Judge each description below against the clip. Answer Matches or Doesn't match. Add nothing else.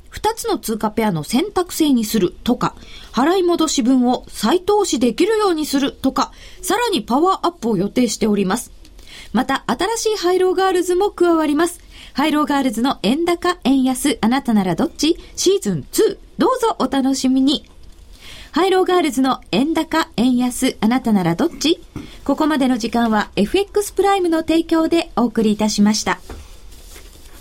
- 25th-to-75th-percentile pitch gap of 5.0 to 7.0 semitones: Doesn't match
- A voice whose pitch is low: Doesn't match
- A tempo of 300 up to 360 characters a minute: Matches